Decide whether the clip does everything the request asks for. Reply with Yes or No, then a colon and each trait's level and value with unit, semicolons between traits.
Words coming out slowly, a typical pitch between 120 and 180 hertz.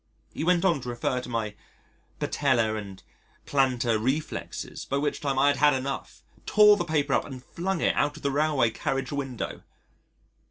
No: average, 175 wpm; medium, 140 Hz